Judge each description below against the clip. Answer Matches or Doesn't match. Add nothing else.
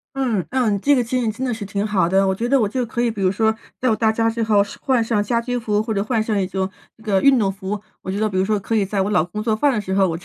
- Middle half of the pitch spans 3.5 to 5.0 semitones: Doesn't match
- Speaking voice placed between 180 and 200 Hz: Doesn't match